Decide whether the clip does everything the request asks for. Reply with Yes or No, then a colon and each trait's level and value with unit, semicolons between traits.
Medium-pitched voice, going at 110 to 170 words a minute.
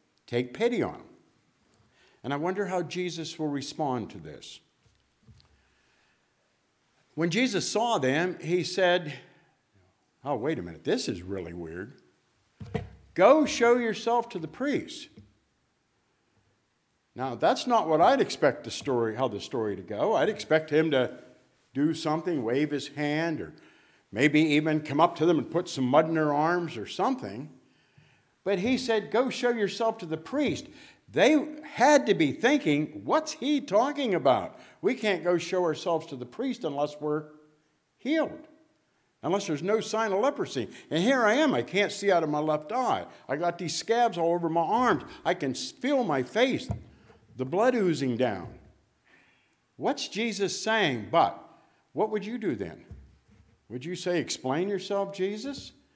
Yes: medium, 175 Hz; average, 160 wpm